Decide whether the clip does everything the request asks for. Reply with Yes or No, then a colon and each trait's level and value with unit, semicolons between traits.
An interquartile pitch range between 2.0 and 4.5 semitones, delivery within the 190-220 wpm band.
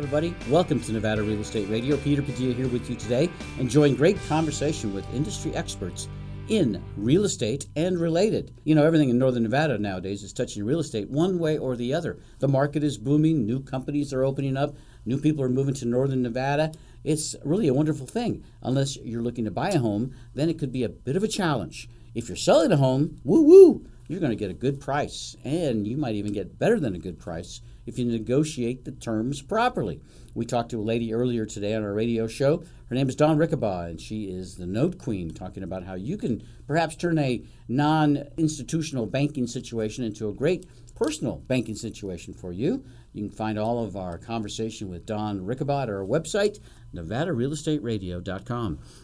No: average, 5.2 semitones; average, 195 wpm